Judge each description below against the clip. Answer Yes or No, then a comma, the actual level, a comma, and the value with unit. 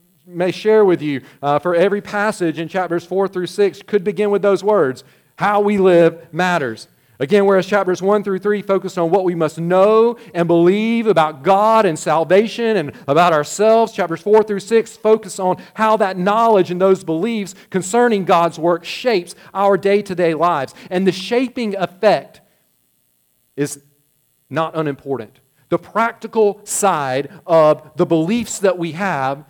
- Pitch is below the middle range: No, medium, 185 Hz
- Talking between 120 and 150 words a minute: No, average, 165 wpm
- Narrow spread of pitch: No, average, 3.8 semitones